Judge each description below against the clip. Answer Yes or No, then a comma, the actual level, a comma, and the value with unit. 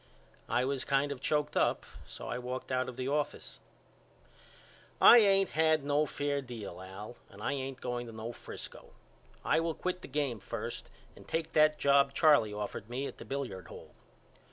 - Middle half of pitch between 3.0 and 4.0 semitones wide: Yes, average, 3.7 semitones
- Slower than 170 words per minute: No, average, 180 wpm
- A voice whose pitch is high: No, low, 135 Hz